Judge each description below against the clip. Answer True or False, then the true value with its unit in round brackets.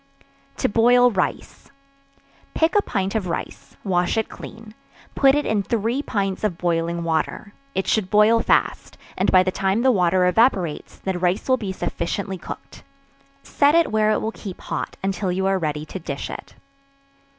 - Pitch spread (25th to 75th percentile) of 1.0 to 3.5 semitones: False (3.9 semitones)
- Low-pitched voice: False (195 Hz)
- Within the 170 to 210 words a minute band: True (175 wpm)